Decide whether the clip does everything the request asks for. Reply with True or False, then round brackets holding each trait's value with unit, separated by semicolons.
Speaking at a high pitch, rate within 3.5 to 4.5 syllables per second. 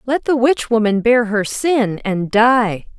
True (230 Hz; 3.6 syllables/s)